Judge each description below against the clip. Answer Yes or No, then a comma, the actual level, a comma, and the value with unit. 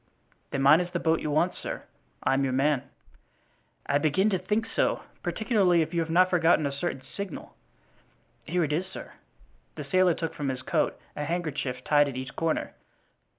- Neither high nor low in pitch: Yes, medium, 160 Hz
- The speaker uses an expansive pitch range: No, average, 4.1 semitones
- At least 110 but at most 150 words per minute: No, average, 190 wpm